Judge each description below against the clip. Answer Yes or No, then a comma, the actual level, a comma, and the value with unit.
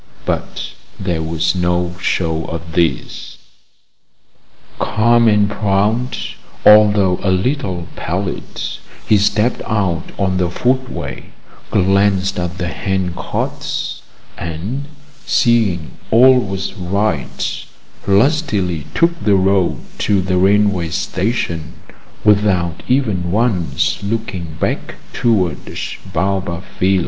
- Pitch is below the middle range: Yes, very low, 95 Hz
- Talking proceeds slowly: Yes, slow, 100 wpm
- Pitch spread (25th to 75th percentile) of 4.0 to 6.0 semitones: No, average, 3.2 semitones